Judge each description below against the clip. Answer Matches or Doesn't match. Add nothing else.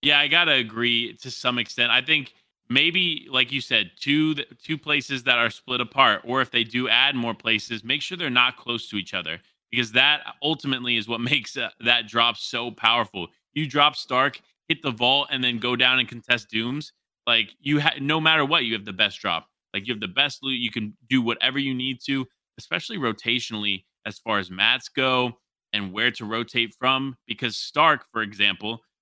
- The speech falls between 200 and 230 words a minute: Matches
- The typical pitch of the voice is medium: Doesn't match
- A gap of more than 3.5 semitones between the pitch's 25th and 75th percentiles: Doesn't match